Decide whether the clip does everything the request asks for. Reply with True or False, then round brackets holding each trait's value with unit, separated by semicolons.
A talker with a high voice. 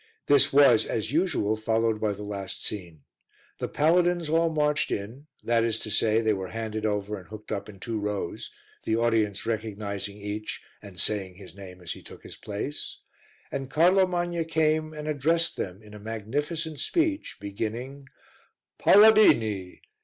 False (110 Hz)